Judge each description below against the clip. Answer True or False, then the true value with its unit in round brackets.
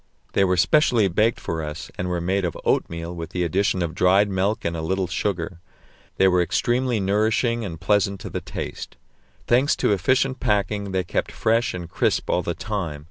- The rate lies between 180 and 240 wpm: True (190 wpm)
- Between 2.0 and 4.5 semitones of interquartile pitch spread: True (3.6 semitones)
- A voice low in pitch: True (95 Hz)